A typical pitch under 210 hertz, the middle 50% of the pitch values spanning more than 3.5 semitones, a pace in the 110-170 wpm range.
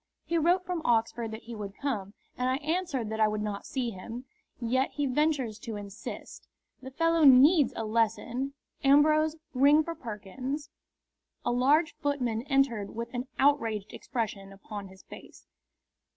No: very high, 250 Hz; average, 4.8 semitones; average, 155 wpm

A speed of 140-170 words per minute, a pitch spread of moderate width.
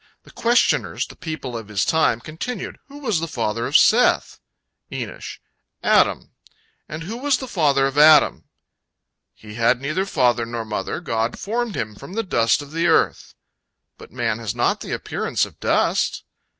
No: average, 155 wpm; wide, 8.1 semitones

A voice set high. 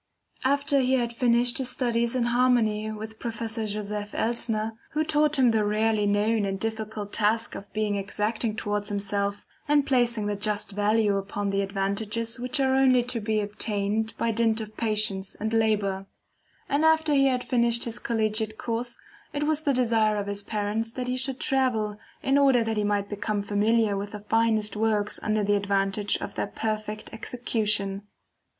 Yes: high, 220 Hz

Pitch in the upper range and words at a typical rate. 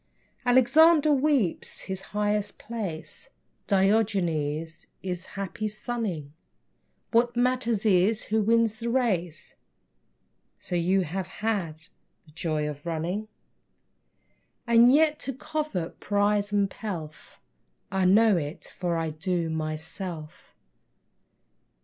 No: high, 195 Hz; slow, 105 wpm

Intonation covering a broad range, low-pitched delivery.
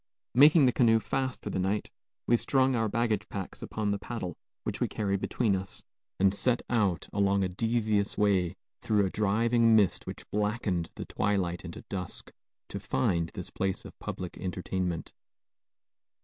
No: average, 3.4 semitones; low, 100 Hz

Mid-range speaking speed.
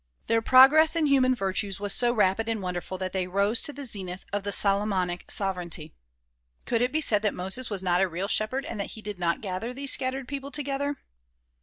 No: fast, 210 wpm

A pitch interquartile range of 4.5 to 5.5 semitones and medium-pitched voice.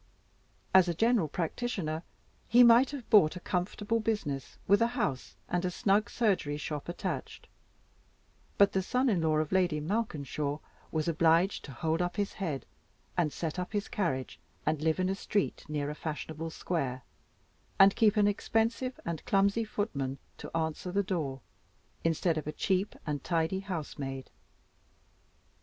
Yes: average, 4.9 semitones; medium, 175 Hz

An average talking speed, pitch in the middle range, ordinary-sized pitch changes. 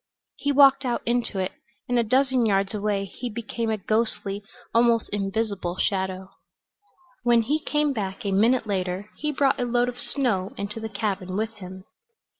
No: average, 170 wpm; high, 220 Hz; average, 3.8 semitones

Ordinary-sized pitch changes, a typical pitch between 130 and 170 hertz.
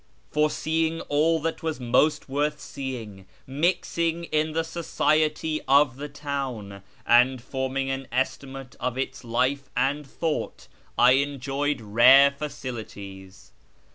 Yes: average, 3.1 semitones; medium, 140 Hz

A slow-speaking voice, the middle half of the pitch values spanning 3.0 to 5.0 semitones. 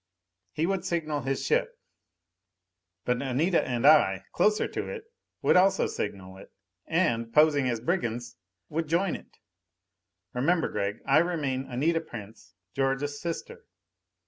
No: slow, 130 wpm; wide, 5.6 semitones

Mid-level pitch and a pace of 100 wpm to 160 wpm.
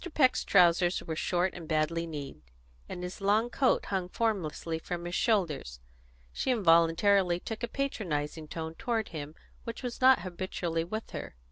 Yes: medium, 180 Hz; average, 155 wpm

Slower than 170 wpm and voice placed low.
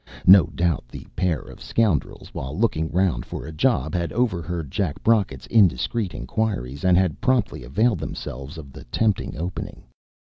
Yes: average, 160 wpm; very low, 90 Hz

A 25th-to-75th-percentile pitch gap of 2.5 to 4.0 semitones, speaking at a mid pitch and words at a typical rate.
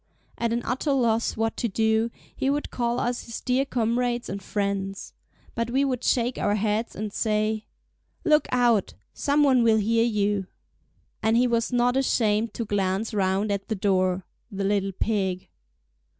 No: average, 3.1 semitones; high, 225 Hz; average, 165 wpm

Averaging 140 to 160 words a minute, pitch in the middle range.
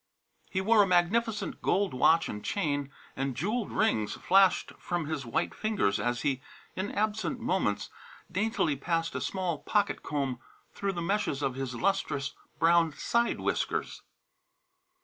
Yes: average, 145 wpm; medium, 170 Hz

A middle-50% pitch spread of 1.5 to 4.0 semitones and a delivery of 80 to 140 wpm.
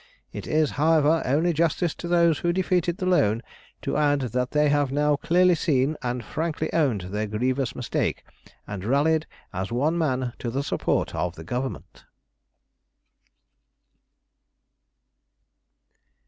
No: average, 4.5 semitones; slow, 135 wpm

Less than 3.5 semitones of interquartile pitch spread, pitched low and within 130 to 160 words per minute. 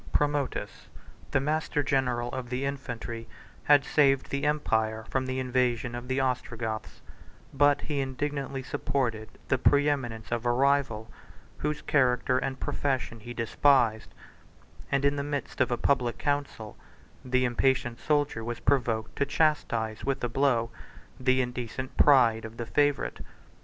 Yes: average, 2.9 semitones; low, 130 Hz; average, 140 wpm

